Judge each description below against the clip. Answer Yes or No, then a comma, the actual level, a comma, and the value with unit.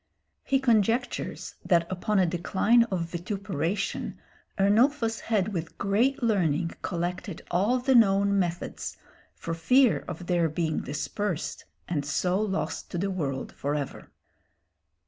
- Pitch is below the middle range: No, high, 190 Hz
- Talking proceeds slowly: Yes, slow, 125 wpm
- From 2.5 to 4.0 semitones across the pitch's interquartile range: No, average, 4.4 semitones